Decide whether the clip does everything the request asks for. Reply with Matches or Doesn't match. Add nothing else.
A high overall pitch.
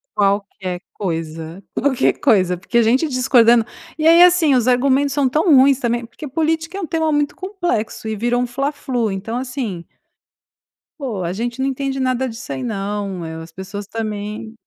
Matches